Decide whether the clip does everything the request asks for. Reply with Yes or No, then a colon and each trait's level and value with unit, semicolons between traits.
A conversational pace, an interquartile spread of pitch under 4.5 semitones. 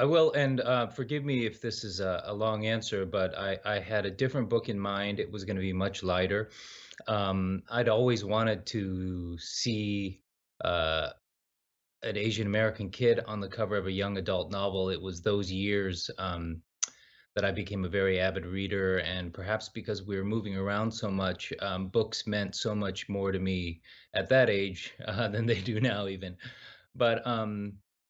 Yes: average, 190 wpm; average, 2.7 semitones